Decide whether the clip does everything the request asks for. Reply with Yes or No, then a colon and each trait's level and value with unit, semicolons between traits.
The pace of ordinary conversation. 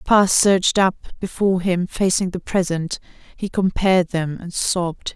Yes: average, 165 wpm